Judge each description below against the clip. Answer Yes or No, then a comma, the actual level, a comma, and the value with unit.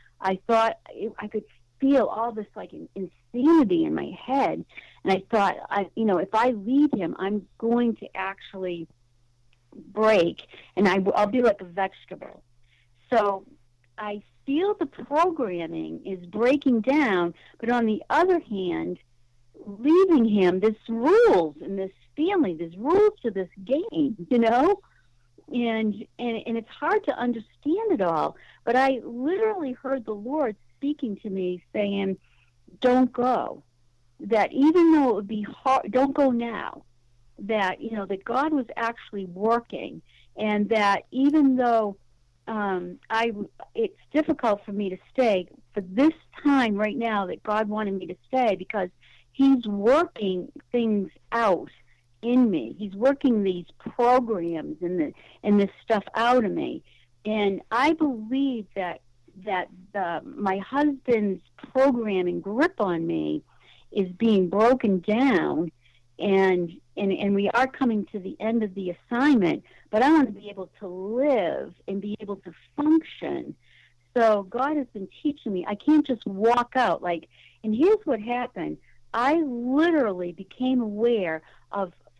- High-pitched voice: Yes, high, 215 Hz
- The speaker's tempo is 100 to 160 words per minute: Yes, average, 150 wpm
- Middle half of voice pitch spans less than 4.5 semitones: No, wide, 5.6 semitones